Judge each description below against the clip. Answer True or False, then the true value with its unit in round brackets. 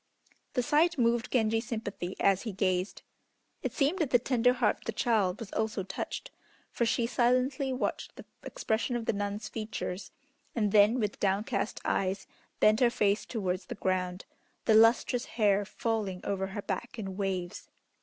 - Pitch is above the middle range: True (220 Hz)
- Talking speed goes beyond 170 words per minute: False (165 wpm)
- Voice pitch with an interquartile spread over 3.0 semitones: True (3.5 semitones)